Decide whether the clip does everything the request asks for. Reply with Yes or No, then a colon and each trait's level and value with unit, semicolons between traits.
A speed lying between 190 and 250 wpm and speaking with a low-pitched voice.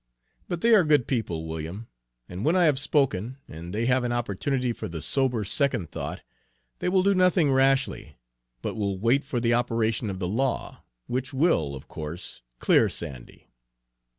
No: average, 175 wpm; low, 120 Hz